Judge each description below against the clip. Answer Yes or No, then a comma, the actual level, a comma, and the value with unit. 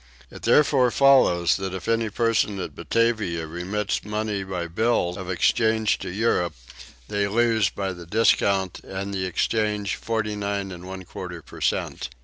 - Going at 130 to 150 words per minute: Yes, average, 140 wpm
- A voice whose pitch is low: Yes, low, 100 Hz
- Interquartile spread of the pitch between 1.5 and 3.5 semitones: Yes, average, 3.2 semitones